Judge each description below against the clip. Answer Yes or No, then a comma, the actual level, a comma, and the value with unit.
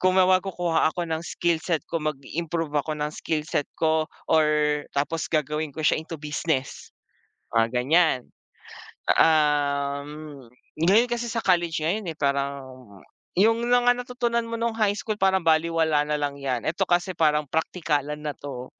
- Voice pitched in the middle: Yes, medium, 160 Hz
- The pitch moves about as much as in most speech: Yes, average, 3.7 semitones